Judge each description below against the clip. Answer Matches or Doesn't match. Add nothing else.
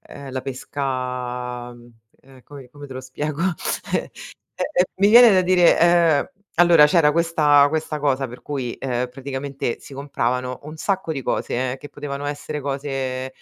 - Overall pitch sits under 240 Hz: Matches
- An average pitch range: Matches